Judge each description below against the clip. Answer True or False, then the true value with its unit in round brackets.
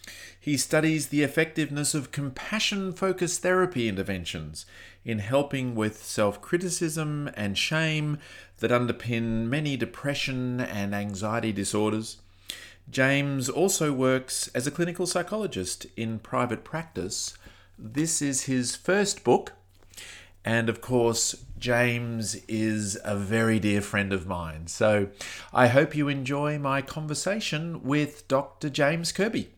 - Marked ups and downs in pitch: True (6.2 semitones)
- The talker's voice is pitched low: True (125 Hz)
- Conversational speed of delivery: False (120 wpm)